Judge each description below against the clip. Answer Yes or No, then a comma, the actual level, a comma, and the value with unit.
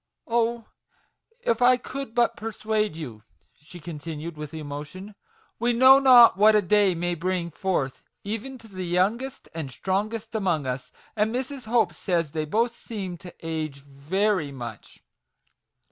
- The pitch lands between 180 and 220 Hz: Yes, high, 190 Hz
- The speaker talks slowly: No, average, 160 wpm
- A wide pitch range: Yes, wide, 6.4 semitones